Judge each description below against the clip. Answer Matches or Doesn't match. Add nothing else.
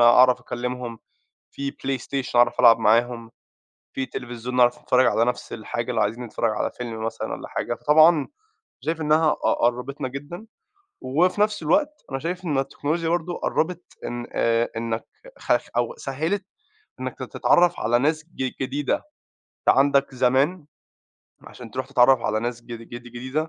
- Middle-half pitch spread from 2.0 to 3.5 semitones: Doesn't match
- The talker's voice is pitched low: Matches